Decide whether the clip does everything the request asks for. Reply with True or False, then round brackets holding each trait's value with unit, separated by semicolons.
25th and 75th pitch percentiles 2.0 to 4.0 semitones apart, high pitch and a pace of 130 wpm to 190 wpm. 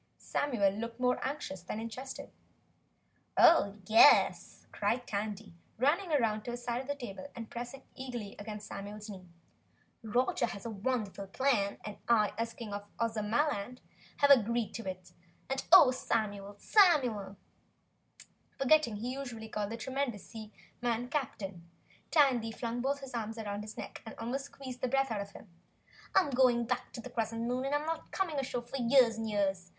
True (3.7 semitones; 230 Hz; 165 wpm)